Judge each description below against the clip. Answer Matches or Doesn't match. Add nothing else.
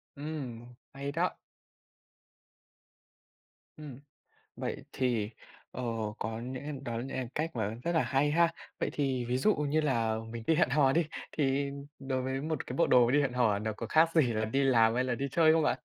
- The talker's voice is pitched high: Doesn't match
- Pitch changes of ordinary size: Matches